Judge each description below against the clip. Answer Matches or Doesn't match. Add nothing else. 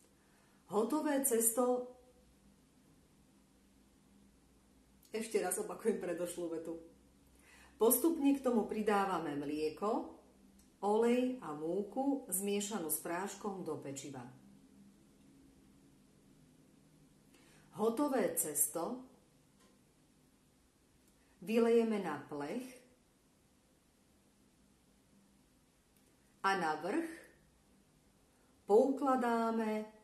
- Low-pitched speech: Doesn't match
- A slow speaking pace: Matches